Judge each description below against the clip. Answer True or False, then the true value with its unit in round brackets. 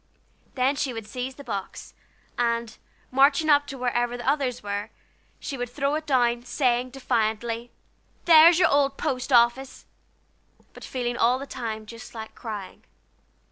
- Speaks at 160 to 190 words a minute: False (150 wpm)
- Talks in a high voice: True (250 Hz)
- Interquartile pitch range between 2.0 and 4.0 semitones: True (2.8 semitones)